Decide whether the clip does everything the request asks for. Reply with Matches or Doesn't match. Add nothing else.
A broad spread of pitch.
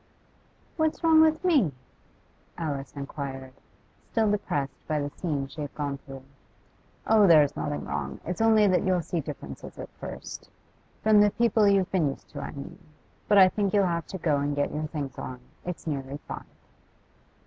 Matches